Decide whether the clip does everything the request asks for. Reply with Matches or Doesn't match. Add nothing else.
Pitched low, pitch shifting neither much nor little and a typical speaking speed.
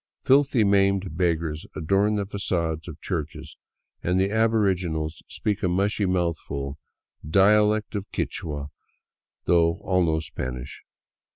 Doesn't match